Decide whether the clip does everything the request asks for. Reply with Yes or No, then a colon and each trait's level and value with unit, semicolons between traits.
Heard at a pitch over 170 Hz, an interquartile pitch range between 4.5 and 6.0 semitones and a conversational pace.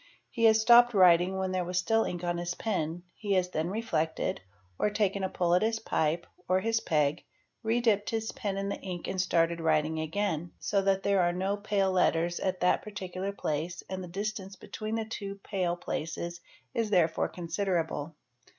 No: medium, 185 Hz; average, 3.1 semitones; average, 190 wpm